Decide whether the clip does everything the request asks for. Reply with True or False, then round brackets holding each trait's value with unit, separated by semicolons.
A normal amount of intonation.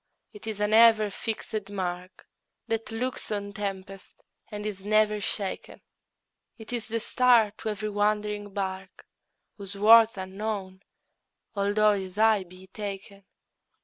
False (1.8 semitones)